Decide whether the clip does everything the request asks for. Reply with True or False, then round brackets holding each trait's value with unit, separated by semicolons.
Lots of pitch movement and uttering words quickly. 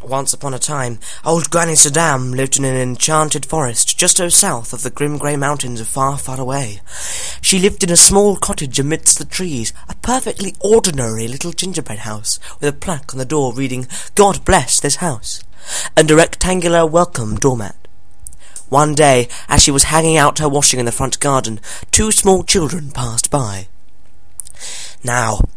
False (5.7 semitones; 170 wpm)